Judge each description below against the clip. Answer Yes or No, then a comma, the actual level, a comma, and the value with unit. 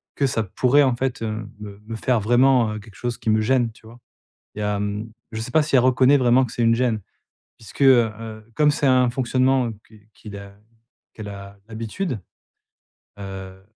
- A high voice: No, low, 115 Hz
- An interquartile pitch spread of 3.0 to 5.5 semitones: Yes, average, 3.3 semitones